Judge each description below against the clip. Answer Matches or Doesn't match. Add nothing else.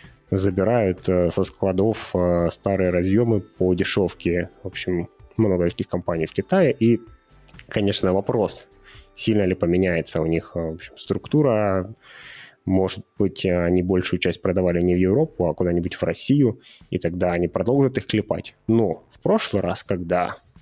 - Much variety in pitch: Doesn't match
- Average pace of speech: Matches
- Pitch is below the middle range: Matches